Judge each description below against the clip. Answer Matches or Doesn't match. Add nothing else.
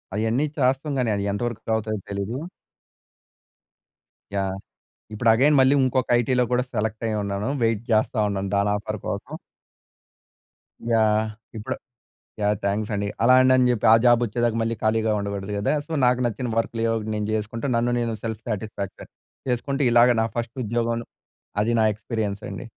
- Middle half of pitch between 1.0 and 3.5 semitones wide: Matches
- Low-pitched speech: Matches